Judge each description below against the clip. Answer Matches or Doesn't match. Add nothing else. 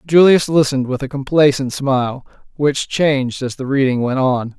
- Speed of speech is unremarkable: Matches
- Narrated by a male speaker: Matches